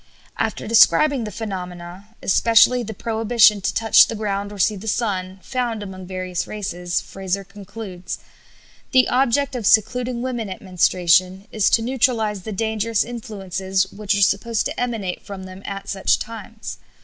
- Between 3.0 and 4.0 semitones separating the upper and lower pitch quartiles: Yes, average, 3.3 semitones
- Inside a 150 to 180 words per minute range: Yes, average, 155 wpm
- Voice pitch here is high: Yes, high, 210 Hz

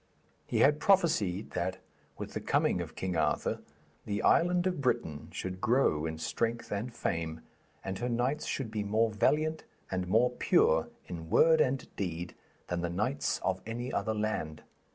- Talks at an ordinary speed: Yes, average, 165 wpm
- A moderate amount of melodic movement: No, wide, 6.2 semitones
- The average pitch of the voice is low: Yes, low, 110 Hz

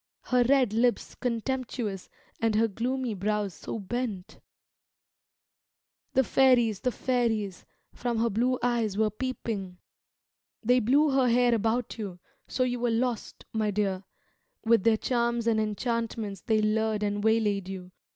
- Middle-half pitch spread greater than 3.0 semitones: No, average, 2.7 semitones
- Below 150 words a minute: Yes, average, 140 wpm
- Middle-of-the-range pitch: No, high, 225 Hz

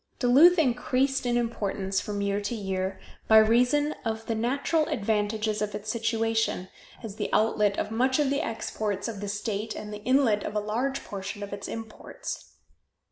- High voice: Yes, high, 220 Hz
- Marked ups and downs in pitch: No, average, 3.1 semitones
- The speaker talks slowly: No, average, 175 wpm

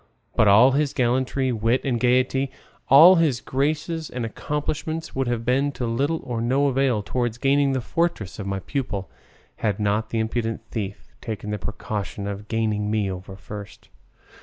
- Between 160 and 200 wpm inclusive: Yes, average, 165 wpm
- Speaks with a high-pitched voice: No, low, 120 Hz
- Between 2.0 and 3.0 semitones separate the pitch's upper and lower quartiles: No, average, 4.4 semitones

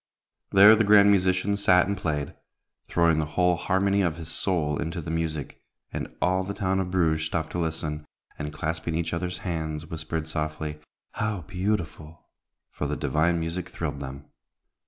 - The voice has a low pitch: Yes, very low, 85 Hz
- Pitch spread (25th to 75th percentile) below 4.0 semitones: Yes, average, 3.1 semitones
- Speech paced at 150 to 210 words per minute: Yes, average, 165 wpm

